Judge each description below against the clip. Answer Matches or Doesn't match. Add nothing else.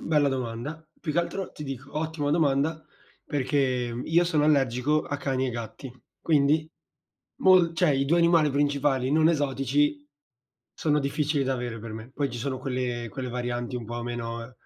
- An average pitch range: Matches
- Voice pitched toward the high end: Doesn't match